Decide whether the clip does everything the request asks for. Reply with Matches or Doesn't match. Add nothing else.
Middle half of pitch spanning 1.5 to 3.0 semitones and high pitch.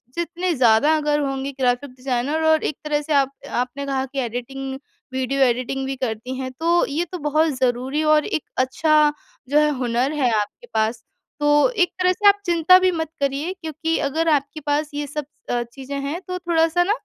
Doesn't match